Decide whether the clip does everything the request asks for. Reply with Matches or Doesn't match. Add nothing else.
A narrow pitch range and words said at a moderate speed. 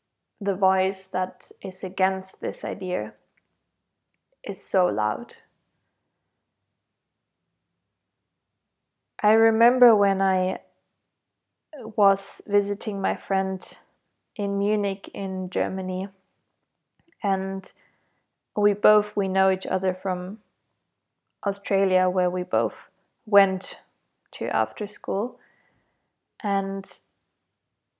Doesn't match